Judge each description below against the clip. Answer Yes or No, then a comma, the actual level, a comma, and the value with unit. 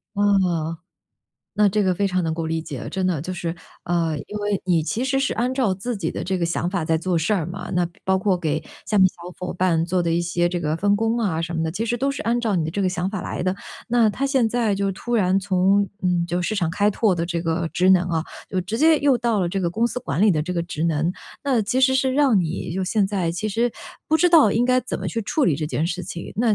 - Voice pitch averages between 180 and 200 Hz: Yes, medium, 185 Hz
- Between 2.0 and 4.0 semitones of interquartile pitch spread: No, average, 4.5 semitones